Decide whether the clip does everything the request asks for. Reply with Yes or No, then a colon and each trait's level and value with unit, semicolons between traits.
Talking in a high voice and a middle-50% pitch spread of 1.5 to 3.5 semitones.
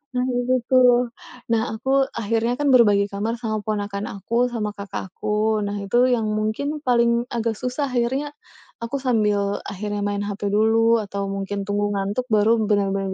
Yes: high, 220 Hz; average, 2.7 semitones